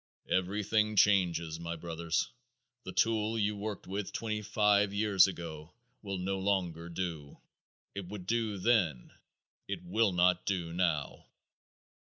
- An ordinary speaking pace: No, slow, 130 wpm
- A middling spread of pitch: Yes, average, 3.5 semitones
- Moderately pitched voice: No, very low, 95 Hz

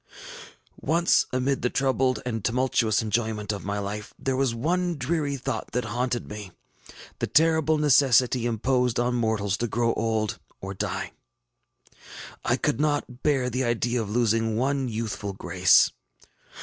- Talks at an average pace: Yes, average, 150 wpm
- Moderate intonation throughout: Yes, average, 3.4 semitones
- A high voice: No, low, 120 Hz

